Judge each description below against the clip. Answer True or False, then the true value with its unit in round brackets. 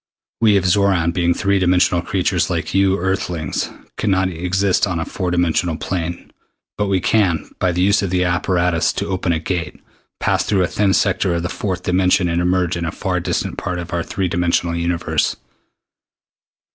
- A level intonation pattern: True (1.7 semitones)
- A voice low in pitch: True (90 Hz)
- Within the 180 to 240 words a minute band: True (185 wpm)